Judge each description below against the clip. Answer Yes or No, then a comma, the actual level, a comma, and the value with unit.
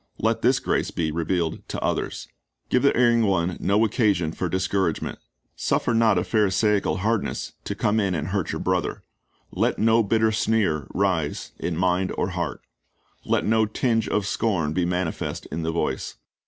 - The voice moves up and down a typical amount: Yes, average, 4.2 semitones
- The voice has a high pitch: No, very low, 95 Hz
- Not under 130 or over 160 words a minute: No, average, 170 wpm